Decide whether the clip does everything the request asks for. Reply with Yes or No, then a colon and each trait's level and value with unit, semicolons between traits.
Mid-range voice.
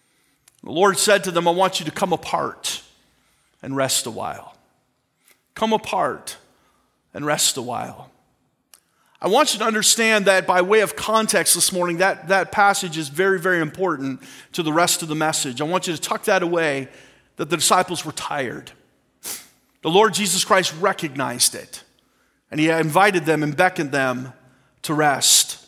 Yes: medium, 175 Hz